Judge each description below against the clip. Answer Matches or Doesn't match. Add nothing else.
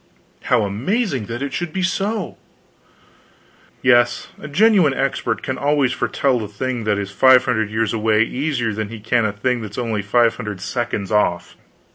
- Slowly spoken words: Doesn't match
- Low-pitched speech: Matches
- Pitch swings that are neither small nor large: Matches